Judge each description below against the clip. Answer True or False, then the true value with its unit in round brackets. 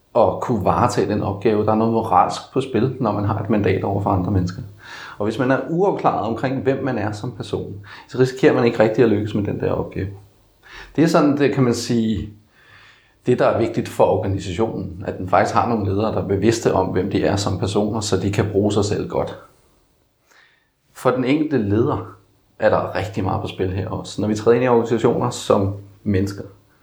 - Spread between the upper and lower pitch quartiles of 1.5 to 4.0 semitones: True (3.2 semitones)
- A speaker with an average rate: True (215 wpm)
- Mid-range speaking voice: False (105 Hz)